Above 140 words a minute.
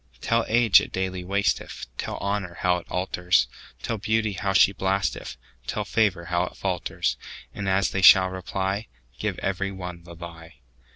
No: slow, 135 wpm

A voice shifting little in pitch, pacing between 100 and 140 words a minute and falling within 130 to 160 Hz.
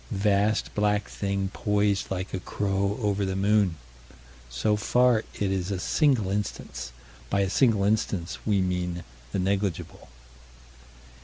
No: narrow, 1.6 semitones; slow, 135 wpm; low, 100 Hz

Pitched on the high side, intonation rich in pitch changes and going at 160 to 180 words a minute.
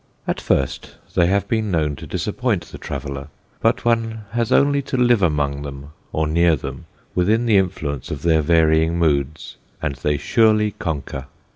No: very low, 80 Hz; wide, 6.9 semitones; average, 165 wpm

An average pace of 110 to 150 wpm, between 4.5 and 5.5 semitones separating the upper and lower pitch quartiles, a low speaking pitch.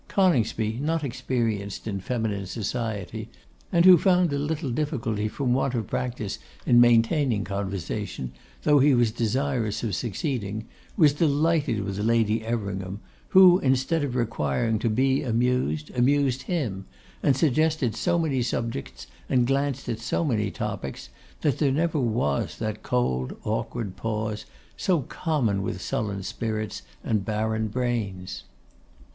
Yes: slow, 135 wpm; average, 4.8 semitones; low, 120 Hz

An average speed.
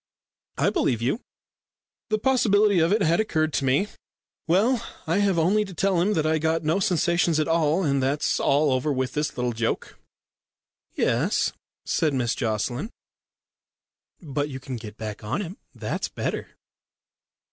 Yes: average, 160 wpm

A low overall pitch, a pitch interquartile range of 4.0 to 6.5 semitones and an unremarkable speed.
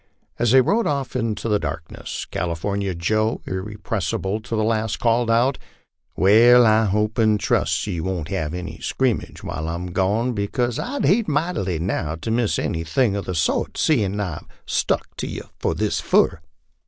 Yes: low, 105 Hz; average, 4.6 semitones; average, 170 wpm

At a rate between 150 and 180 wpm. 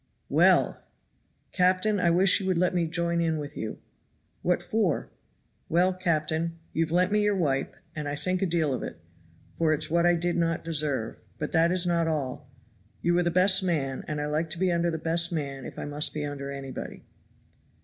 No: average, 200 wpm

